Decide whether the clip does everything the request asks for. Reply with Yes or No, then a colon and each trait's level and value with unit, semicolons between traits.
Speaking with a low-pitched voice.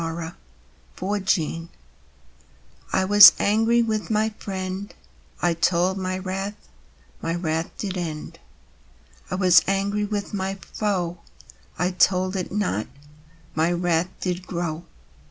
No: medium, 185 Hz